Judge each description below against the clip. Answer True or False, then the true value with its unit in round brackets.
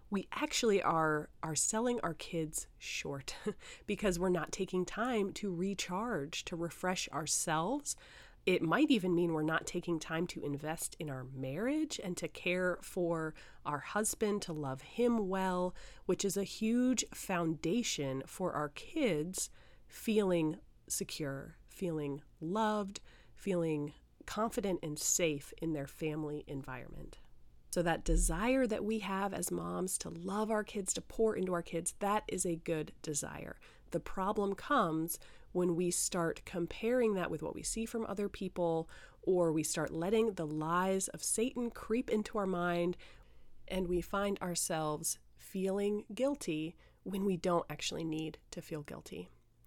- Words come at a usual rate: True (150 wpm)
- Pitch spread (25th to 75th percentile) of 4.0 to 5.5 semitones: True (4.6 semitones)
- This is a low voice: False (180 Hz)